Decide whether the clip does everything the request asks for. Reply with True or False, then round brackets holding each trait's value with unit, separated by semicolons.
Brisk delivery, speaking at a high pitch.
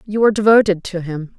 True (215 wpm; 195 Hz)